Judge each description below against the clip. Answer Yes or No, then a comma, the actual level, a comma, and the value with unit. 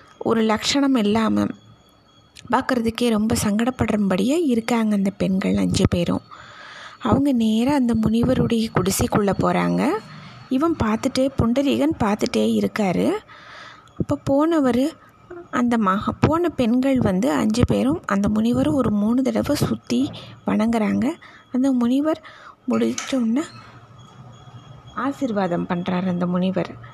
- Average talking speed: Yes, average, 100 wpm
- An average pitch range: No, wide, 6.2 semitones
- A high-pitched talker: Yes, high, 225 Hz